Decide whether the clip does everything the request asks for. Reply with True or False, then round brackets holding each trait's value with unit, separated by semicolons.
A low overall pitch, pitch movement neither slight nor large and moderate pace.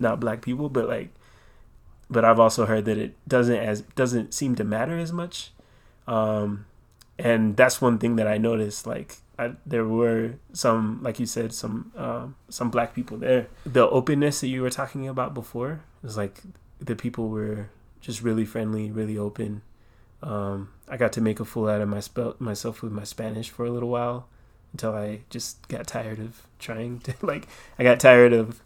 False (115 Hz; 2.2 semitones; 195 wpm)